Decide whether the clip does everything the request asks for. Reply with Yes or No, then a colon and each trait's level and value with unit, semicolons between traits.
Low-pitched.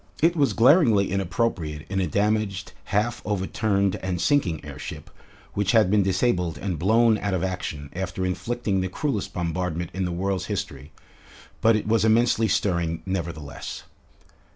Yes: very low, 95 Hz